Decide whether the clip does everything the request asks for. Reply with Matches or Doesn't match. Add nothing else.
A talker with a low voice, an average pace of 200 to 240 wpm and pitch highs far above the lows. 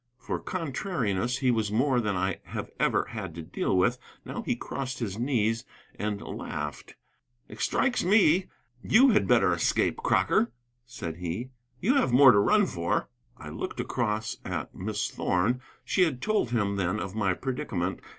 Doesn't match